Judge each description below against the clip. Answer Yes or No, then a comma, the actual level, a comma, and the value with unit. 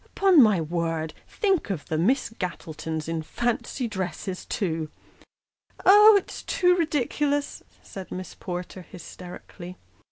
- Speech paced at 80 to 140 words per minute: Yes, slow, 135 wpm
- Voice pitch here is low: No, high, 190 Hz